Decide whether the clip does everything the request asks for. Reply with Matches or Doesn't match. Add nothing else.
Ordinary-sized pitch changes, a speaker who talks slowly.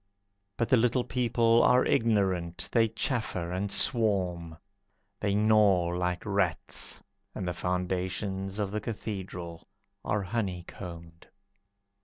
Matches